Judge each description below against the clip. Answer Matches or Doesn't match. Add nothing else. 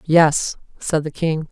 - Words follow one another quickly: Doesn't match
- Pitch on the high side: Doesn't match